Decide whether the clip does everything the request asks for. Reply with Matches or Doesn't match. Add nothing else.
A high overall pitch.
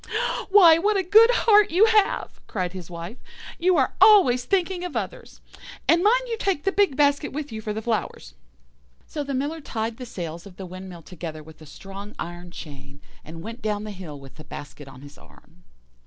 Matches